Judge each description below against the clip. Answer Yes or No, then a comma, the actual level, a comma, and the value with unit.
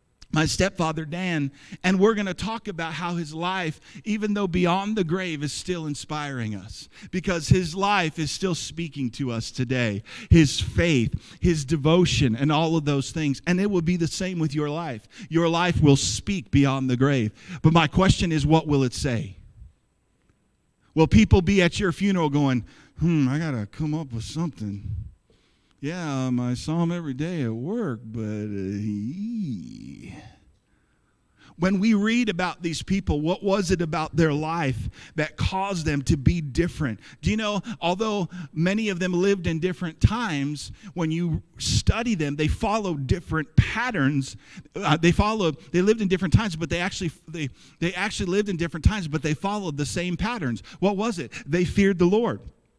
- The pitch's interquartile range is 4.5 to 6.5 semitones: Yes, average, 5.0 semitones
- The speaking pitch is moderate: Yes, medium, 160 Hz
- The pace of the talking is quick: No, average, 175 wpm